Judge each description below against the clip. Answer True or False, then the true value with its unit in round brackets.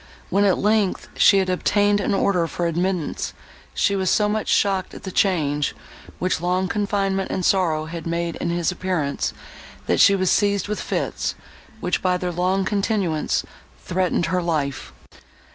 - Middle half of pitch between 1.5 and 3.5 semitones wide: True (2.6 semitones)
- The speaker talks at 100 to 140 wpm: False (160 wpm)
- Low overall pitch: False (185 Hz)